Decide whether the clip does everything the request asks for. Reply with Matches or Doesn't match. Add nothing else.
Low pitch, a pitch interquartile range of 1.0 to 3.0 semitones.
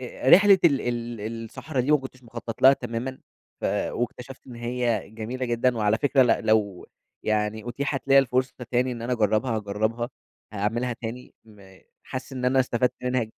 Matches